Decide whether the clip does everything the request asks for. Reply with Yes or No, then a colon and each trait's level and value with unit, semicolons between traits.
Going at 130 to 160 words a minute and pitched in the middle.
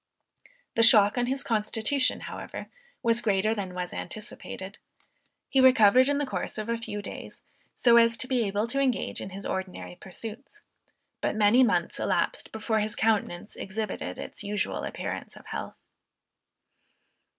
No: average, 150 wpm; high, 220 Hz